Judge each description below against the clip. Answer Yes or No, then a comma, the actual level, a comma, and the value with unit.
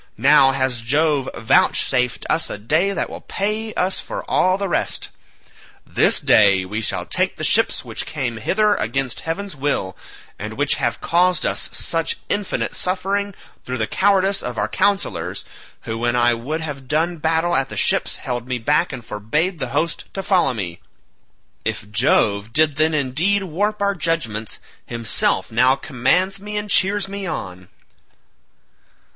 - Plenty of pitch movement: Yes, wide, 7.8 semitones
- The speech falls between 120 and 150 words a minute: No, average, 160 wpm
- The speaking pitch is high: No, medium, 150 Hz